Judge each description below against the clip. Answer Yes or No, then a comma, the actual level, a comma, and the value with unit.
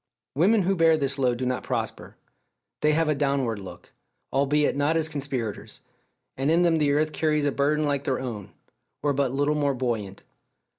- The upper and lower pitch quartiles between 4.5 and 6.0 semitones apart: No, narrow, 2.6 semitones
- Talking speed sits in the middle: Yes, average, 185 wpm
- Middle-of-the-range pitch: Yes, medium, 145 Hz